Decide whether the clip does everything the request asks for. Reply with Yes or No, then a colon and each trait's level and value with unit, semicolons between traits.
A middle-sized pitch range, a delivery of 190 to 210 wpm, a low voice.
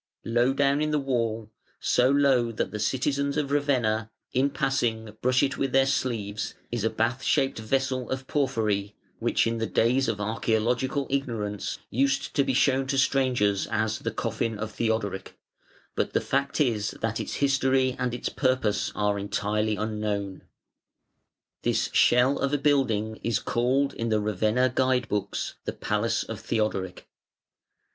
No: average, 3.8 semitones; average, 155 wpm; low, 120 Hz